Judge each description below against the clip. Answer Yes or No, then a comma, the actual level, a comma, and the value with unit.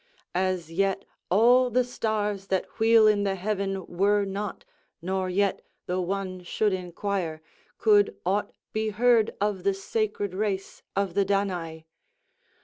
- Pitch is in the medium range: No, high, 200 Hz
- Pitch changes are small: Yes, narrow, 2.1 semitones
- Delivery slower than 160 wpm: Yes, average, 140 wpm